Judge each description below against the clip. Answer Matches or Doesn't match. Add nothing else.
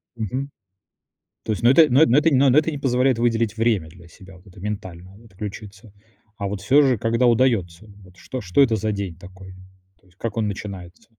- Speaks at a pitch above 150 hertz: Doesn't match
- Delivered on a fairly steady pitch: Doesn't match